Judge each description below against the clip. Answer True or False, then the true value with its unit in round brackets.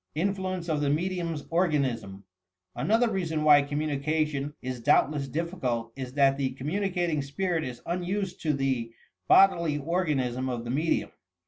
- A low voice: False (150 Hz)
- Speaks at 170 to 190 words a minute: False (145 wpm)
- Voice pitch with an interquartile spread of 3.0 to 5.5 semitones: True (4.4 semitones)